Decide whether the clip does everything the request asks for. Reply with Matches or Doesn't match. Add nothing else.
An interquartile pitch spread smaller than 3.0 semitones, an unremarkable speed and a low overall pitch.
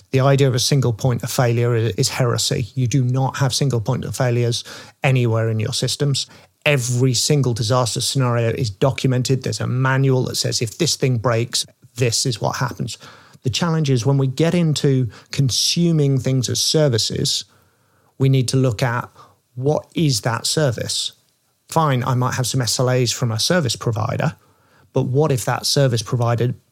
Matches